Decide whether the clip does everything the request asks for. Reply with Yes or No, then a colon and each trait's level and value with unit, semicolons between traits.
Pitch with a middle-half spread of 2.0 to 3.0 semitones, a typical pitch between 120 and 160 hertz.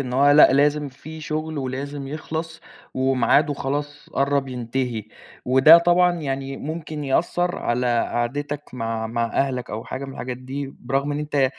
Yes: narrow, 2.5 semitones; medium, 140 Hz